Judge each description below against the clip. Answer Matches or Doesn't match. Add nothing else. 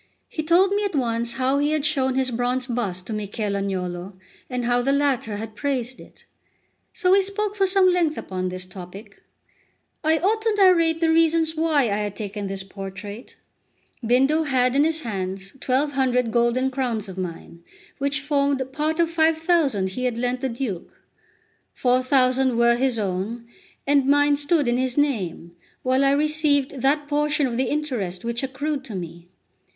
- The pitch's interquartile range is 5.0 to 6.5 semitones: Matches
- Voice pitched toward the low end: Doesn't match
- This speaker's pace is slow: Doesn't match